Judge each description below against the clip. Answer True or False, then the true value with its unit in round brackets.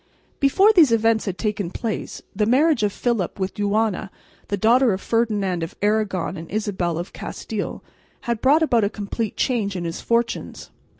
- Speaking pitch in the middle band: False (215 Hz)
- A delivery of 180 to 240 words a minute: False (170 wpm)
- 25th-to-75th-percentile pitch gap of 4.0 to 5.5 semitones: False (3.3 semitones)